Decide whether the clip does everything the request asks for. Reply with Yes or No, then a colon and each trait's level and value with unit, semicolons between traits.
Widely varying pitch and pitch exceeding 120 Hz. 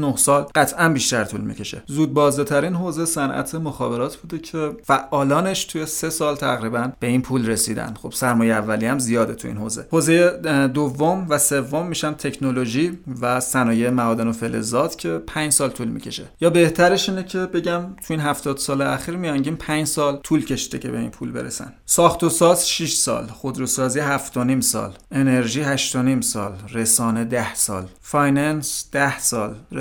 No: average, 4.3 semitones; medium, 140 Hz